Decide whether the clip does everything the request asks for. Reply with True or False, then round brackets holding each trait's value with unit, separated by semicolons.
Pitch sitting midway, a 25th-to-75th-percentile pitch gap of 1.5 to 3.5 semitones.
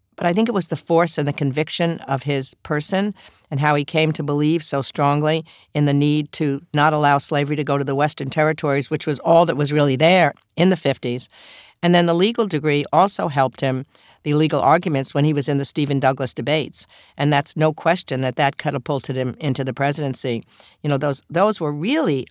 True (150 Hz; 2.5 semitones)